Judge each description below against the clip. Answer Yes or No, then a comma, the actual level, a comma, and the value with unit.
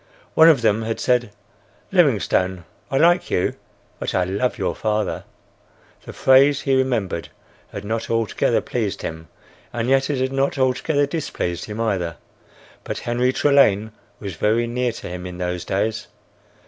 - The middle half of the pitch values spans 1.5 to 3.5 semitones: No, average, 5.3 semitones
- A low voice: Yes, low, 115 Hz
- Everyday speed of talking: Yes, average, 155 wpm